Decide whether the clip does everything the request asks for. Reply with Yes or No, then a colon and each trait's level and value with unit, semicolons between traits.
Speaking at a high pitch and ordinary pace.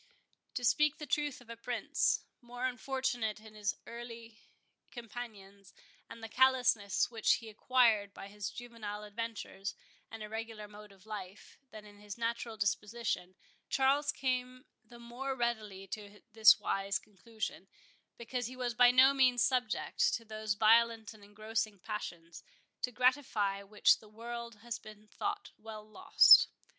Yes: high, 225 Hz; average, 145 wpm